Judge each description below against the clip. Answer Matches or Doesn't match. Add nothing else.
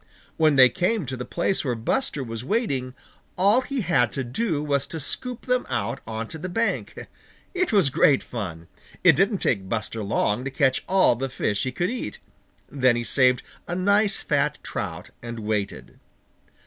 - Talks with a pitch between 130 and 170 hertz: Matches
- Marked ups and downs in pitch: Matches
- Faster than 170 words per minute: Matches